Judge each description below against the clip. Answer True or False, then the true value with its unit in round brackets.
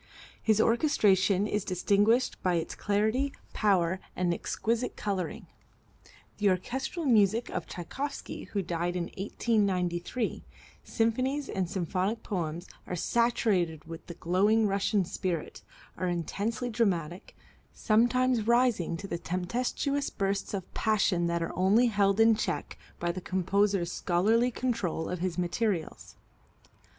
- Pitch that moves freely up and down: False (4.3 semitones)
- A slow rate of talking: True (120 wpm)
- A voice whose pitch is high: True (200 Hz)